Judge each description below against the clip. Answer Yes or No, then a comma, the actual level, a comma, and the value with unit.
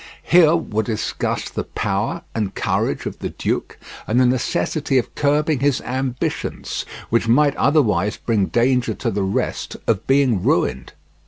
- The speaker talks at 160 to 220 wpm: No, average, 150 wpm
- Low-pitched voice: Yes, low, 125 Hz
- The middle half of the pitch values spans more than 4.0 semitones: Yes, average, 4.5 semitones